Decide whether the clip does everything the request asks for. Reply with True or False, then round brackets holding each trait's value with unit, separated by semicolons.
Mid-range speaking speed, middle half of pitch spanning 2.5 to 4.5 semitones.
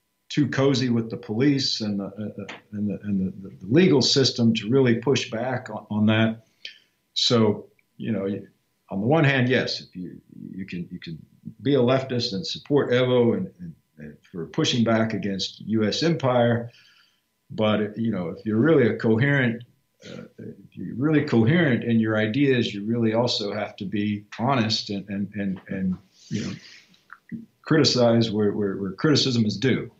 True (175 wpm; 4.1 semitones)